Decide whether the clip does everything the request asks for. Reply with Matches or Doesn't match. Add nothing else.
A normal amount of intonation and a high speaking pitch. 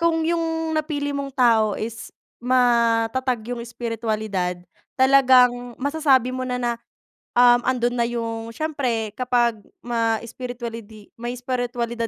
Doesn't match